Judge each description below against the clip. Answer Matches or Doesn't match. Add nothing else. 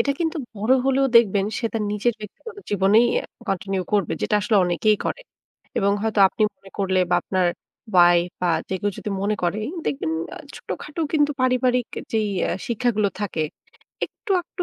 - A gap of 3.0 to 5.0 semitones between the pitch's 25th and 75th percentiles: Matches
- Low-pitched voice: Doesn't match